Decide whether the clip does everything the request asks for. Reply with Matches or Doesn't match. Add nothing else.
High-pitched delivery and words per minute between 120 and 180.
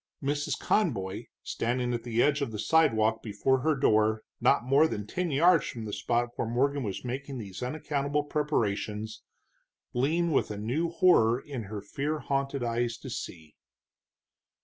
Doesn't match